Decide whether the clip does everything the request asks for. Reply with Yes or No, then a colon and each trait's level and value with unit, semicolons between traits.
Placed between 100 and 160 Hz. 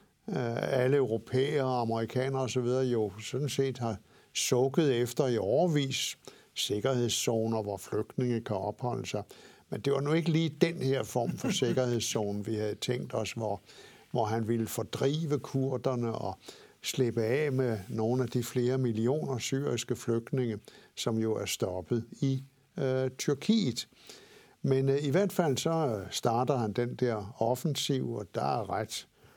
Yes: low, 125 Hz